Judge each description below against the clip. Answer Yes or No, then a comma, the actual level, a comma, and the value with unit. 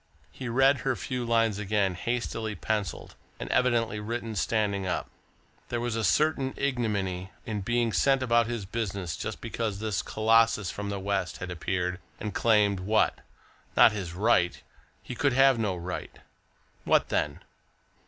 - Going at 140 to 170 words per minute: Yes, average, 155 wpm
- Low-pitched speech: Yes, low, 110 Hz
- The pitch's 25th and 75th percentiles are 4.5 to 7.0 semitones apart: No, average, 3.5 semitones